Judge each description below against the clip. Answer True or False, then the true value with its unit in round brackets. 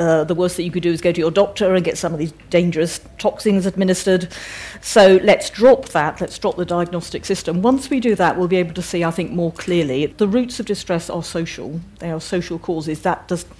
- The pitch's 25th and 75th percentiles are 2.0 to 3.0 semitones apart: True (2.4 semitones)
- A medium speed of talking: False (240 wpm)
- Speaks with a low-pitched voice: False (175 Hz)